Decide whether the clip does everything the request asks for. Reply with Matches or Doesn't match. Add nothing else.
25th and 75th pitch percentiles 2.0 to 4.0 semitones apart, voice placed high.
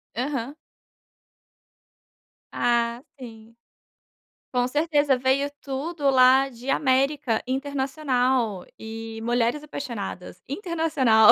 Matches